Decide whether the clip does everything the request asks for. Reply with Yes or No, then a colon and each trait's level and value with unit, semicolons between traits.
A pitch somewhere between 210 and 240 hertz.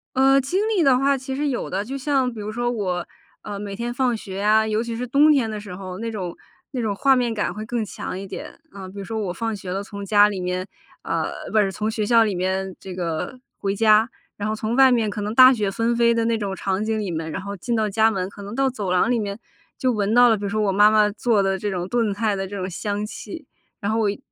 Yes: high, 215 Hz